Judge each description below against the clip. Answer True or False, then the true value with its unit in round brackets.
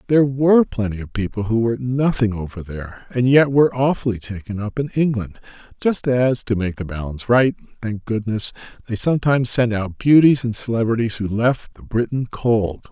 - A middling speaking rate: True (170 wpm)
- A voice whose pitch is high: False (115 Hz)